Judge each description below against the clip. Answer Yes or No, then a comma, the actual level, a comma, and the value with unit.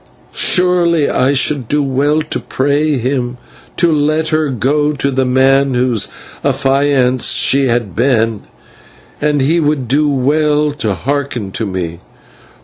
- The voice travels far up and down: No, average, 3.0 semitones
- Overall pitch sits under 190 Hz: Yes, medium, 140 Hz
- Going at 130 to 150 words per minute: Yes, average, 140 wpm